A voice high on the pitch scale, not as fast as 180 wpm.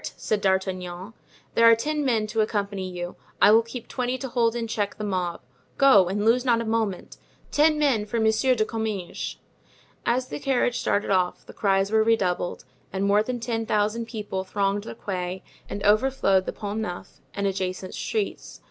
No: high, 215 Hz; average, 185 wpm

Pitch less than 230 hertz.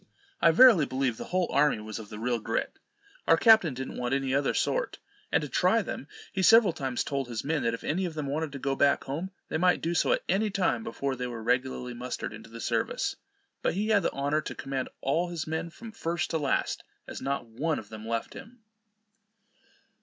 Yes: medium, 140 Hz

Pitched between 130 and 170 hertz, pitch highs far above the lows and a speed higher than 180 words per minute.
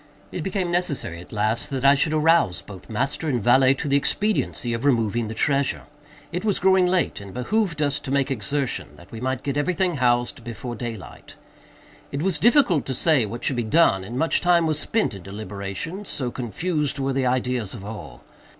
Yes: low, 135 Hz; wide, 5.9 semitones; average, 200 wpm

